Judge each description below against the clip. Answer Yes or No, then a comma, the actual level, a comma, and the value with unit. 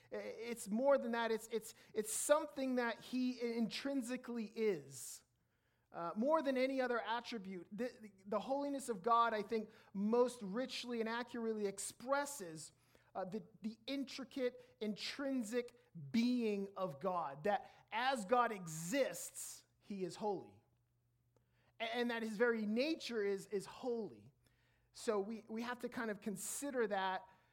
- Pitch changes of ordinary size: Yes, average, 4.0 semitones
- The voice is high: Yes, high, 225 Hz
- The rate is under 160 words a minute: Yes, average, 140 wpm